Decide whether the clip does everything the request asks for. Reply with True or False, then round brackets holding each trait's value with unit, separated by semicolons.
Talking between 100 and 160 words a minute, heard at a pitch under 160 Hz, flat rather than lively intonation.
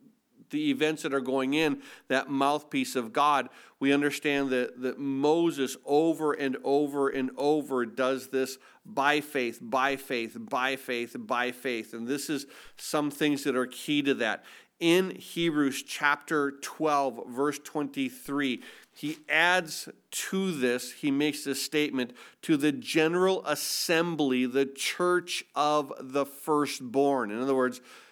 True (140 wpm; 140 Hz; 2.3 semitones)